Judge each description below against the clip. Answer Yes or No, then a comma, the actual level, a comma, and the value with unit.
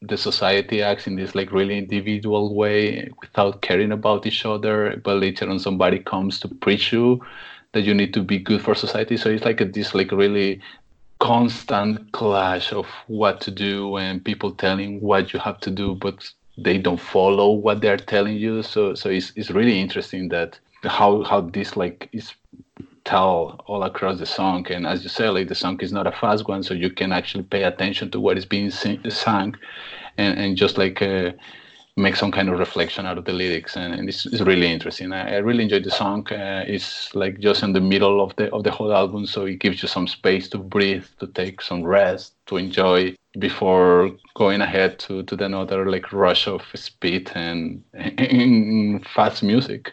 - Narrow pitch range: Yes, narrow, 1.6 semitones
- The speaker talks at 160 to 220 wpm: Yes, average, 200 wpm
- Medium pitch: No, low, 100 Hz